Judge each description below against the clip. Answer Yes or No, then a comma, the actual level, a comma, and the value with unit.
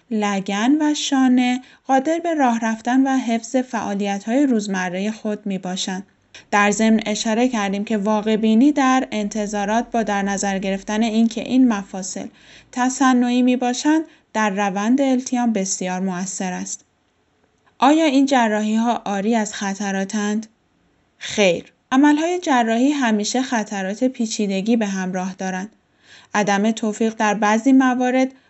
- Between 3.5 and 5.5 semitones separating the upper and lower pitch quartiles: Yes, average, 3.8 semitones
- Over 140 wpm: No, average, 125 wpm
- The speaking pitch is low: No, high, 220 Hz